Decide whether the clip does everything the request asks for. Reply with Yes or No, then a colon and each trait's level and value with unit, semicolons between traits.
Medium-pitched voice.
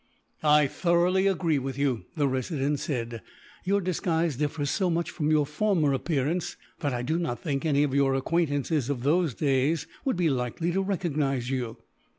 Yes: medium, 150 Hz